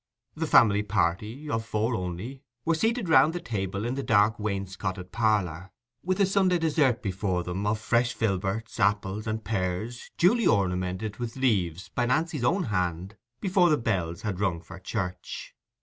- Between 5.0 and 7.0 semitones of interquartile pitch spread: Yes, wide, 5.6 semitones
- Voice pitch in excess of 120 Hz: No, low, 110 Hz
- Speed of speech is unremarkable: Yes, average, 165 wpm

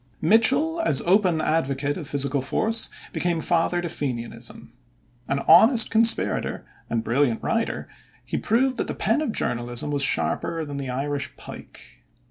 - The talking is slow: No, average, 145 wpm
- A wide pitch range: Yes, wide, 8.0 semitones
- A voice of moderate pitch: Yes, medium, 155 Hz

